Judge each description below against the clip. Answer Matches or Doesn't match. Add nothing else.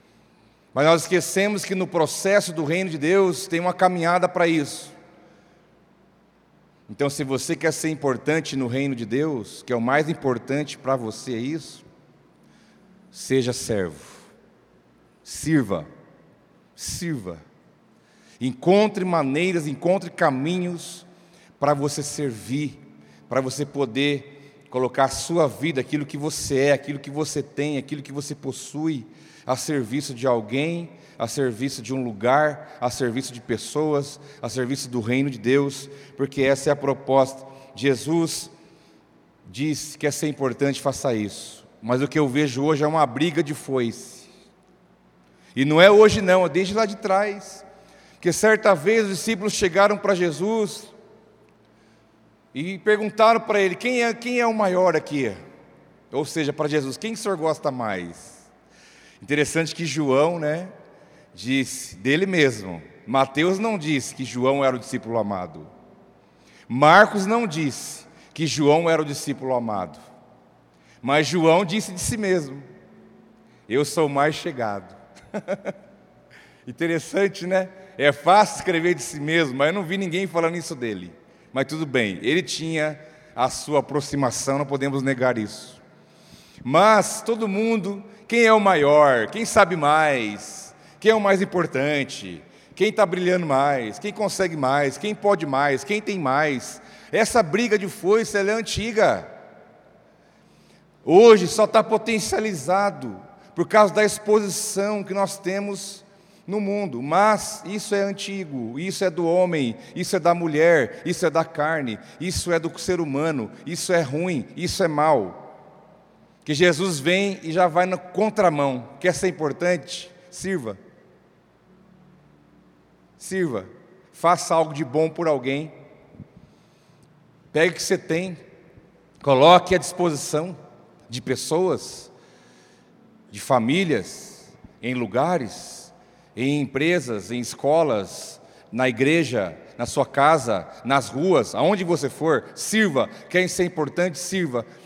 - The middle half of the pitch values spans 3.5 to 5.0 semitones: Doesn't match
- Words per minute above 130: Matches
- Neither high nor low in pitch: Matches